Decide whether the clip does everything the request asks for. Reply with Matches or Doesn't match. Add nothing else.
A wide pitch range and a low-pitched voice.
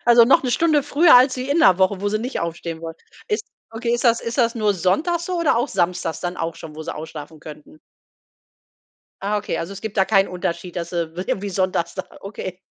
Doesn't match